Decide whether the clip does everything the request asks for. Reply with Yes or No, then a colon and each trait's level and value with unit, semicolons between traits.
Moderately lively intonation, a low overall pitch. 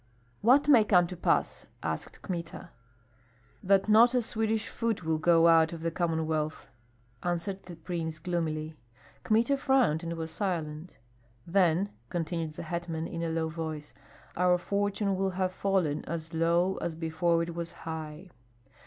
No: average, 3.1 semitones; medium, 170 Hz